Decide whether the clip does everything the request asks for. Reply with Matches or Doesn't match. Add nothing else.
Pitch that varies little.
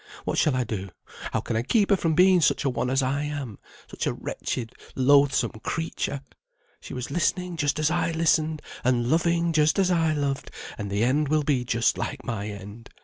Doesn't match